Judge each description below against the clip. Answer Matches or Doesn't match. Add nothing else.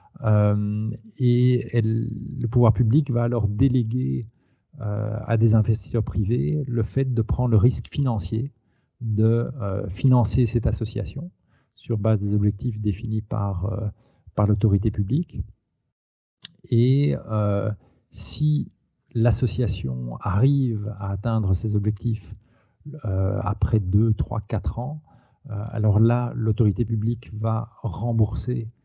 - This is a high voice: Doesn't match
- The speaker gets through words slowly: Matches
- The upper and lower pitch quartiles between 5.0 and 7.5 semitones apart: Doesn't match